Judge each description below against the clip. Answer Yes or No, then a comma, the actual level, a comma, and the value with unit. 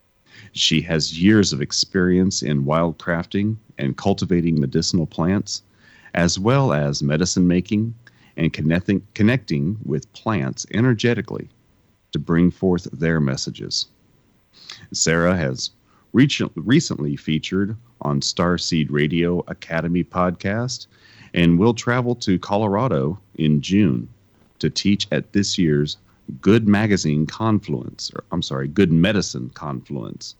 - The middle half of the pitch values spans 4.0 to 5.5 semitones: Yes, average, 4.8 semitones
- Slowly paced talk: Yes, slow, 115 wpm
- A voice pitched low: Yes, very low, 90 Hz